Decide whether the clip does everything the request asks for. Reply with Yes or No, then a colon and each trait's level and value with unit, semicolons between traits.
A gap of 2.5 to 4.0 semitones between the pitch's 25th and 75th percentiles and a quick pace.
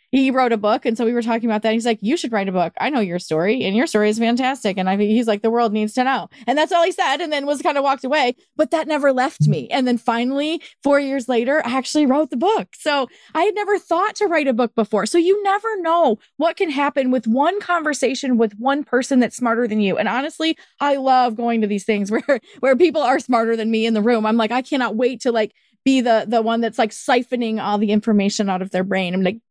No: average, 4.4 semitones; fast, 270 wpm